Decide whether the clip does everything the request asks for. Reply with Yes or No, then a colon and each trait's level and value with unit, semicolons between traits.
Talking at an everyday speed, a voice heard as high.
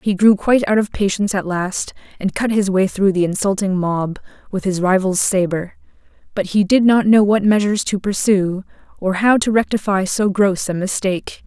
Yes: average, 195 wpm; high, 195 Hz